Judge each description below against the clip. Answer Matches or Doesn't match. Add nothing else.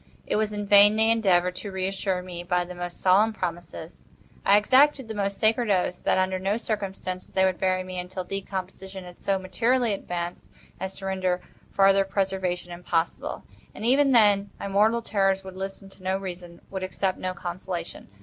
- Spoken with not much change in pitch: Matches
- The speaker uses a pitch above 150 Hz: Matches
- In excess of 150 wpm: Matches